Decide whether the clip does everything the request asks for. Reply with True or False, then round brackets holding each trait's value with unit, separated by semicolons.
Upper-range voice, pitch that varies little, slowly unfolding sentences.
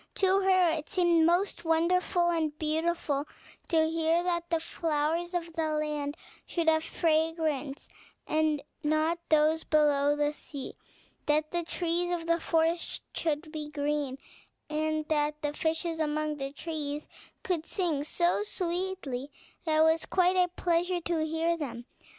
False (320 Hz; 2.2 semitones; 145 wpm)